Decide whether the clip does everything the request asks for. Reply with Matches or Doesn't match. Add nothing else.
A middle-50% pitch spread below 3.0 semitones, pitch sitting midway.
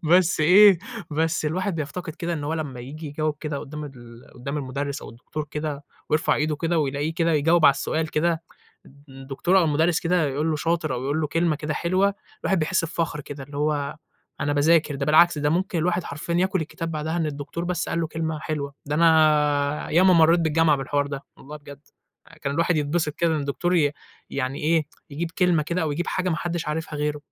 Matches